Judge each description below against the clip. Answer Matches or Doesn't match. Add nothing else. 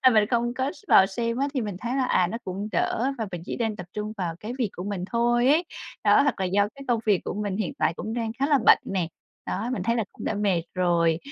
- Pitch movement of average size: Matches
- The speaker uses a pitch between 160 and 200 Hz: Doesn't match